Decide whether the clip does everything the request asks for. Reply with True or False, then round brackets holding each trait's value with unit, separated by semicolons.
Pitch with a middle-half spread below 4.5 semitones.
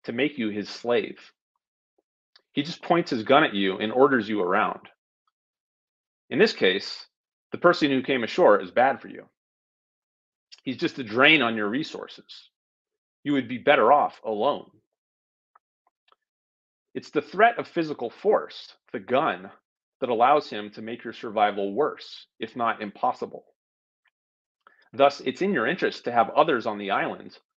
False (5.2 semitones)